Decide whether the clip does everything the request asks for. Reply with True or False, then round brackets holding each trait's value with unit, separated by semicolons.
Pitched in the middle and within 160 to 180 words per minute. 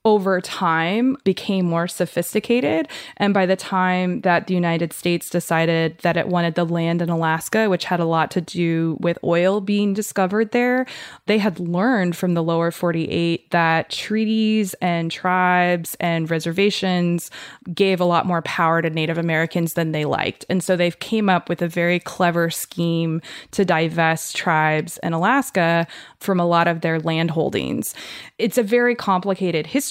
True (175 Hz; 165 wpm)